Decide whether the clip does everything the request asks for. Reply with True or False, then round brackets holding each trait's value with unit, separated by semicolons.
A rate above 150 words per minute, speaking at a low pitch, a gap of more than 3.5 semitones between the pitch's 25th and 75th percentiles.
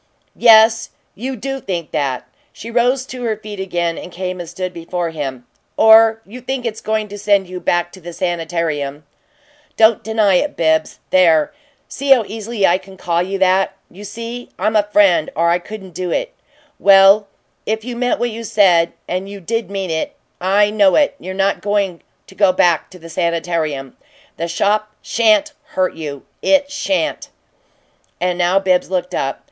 False (175 wpm; 195 Hz; 4.0 semitones)